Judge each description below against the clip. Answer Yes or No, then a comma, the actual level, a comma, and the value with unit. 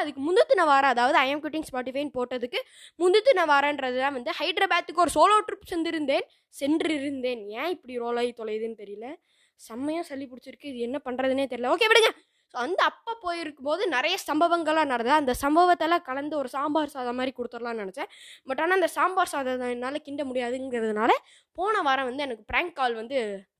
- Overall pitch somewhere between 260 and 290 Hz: Yes, very high, 285 Hz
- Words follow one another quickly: Yes, fast, 165 wpm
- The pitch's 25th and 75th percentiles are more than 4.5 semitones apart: Yes, average, 5.2 semitones